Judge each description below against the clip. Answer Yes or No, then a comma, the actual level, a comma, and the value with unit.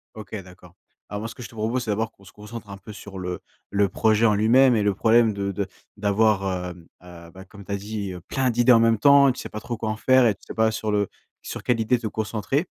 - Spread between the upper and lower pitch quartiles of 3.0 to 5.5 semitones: No, narrow, 2.5 semitones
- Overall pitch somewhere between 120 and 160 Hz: No, low, 105 Hz